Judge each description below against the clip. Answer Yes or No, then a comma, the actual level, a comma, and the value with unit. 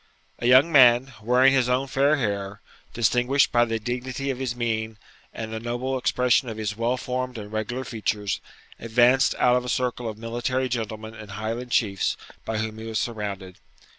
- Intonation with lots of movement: No, narrow, 2.4 semitones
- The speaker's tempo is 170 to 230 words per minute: Yes, average, 180 wpm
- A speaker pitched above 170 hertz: No, low, 120 Hz